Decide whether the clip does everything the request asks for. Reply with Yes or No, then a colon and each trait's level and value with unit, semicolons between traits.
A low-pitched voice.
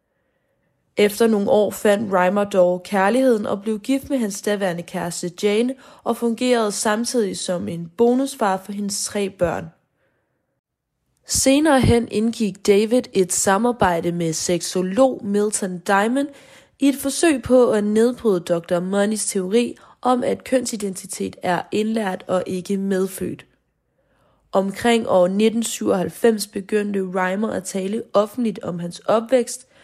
No: high, 205 Hz